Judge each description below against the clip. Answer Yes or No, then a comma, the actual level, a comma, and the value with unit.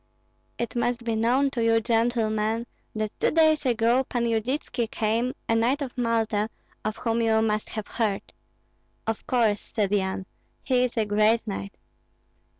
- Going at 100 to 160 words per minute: Yes, average, 155 wpm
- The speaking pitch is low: No, high, 225 Hz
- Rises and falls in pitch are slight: Yes, narrow, 2.1 semitones